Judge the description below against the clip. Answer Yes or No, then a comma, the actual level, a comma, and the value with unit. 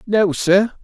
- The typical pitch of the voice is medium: No, high, 200 Hz